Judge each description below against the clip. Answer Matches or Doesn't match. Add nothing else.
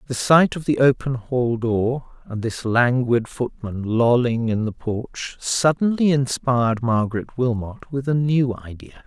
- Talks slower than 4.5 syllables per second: Matches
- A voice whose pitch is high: Doesn't match